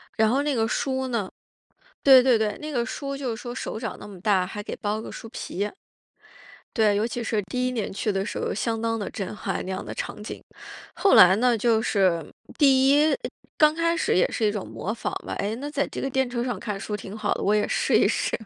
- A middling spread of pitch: Yes, average, 4.0 semitones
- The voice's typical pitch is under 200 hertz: No, high, 225 Hz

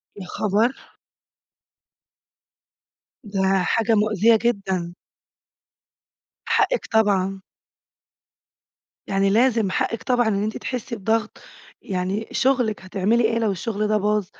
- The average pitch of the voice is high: Yes, high, 215 Hz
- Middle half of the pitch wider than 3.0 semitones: No, average, 2.7 semitones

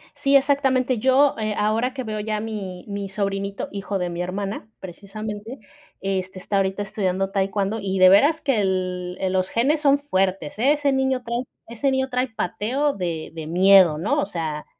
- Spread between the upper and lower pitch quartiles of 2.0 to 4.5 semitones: No, average, 5.1 semitones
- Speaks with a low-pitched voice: No, high, 205 Hz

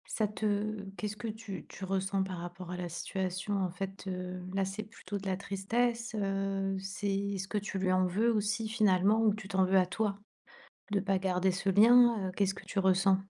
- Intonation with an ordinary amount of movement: No, narrow, 1.9 semitones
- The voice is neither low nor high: No, high, 195 Hz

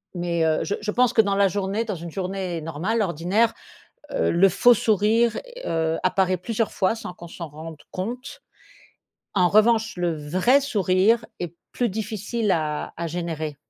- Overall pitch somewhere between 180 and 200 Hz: Yes, high, 190 Hz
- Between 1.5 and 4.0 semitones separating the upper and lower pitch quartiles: No, average, 4.6 semitones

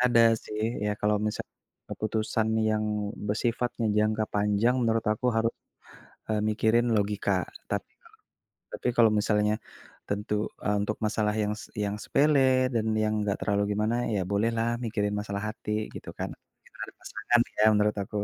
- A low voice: Yes, low, 110 Hz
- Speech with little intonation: Yes, narrow, 1.5 semitones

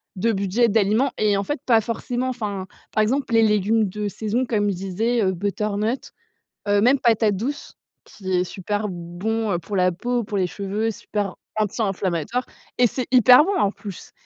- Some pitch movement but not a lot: Yes, average, 3.1 semitones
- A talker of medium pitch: No, high, 210 Hz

